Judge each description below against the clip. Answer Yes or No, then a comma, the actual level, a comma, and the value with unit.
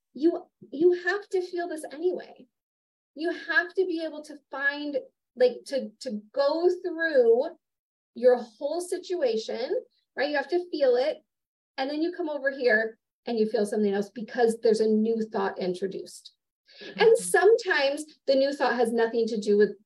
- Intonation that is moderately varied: No, wide, 7.3 semitones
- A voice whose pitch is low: No, very high, 290 Hz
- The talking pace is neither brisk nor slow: Yes, average, 165 wpm